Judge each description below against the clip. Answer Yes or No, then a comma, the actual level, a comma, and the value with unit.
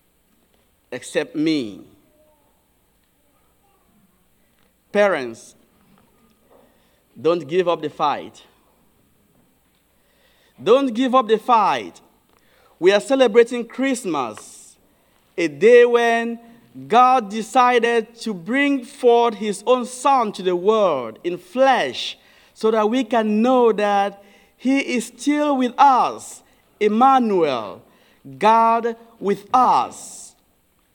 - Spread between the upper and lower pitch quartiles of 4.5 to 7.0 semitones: No, average, 3.9 semitones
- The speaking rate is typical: No, slow, 95 wpm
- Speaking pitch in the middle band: No, high, 235 Hz